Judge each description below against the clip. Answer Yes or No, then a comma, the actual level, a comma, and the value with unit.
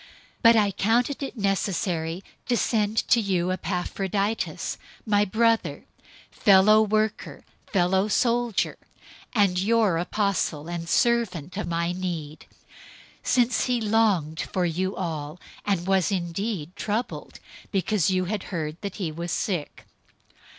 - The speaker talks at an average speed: No, slow, 130 wpm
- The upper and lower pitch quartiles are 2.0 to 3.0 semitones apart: No, average, 3.8 semitones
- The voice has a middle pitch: No, high, 195 Hz